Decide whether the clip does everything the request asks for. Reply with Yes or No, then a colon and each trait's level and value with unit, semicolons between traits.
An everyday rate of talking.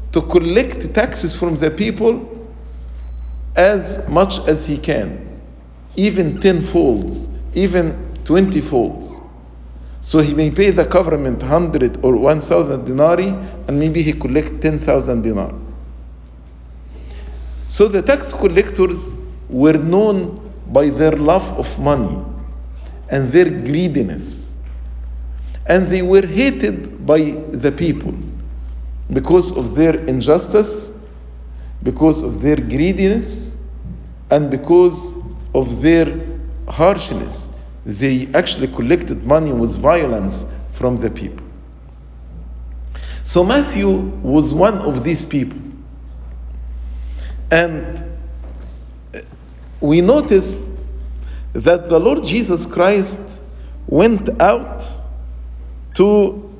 No: slow, 100 wpm